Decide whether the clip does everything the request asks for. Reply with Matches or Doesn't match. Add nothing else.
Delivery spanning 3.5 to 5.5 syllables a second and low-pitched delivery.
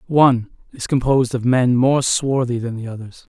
Matches